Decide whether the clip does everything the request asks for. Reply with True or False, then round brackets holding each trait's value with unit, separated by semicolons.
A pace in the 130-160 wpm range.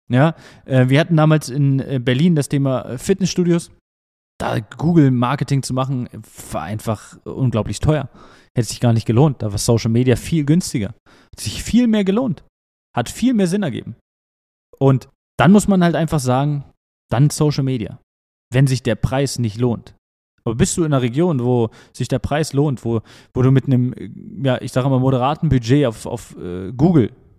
False (175 wpm)